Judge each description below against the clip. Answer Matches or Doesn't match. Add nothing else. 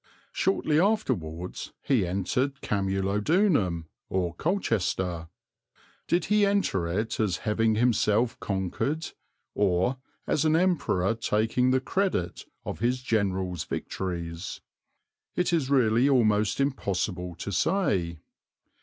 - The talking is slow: Matches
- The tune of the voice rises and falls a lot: Matches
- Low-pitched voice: Matches